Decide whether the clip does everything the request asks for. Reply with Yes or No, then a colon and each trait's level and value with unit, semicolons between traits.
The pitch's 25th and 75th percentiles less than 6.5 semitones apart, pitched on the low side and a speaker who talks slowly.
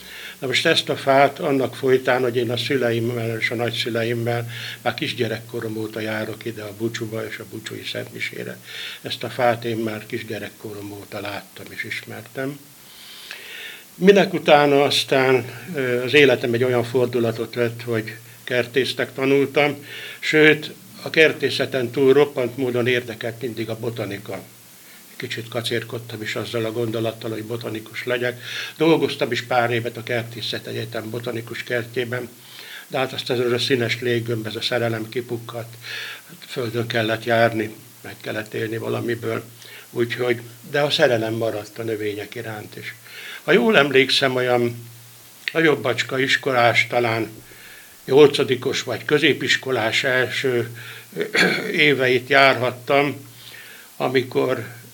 No: narrow, 2.4 semitones; low, 120 Hz; average, 125 wpm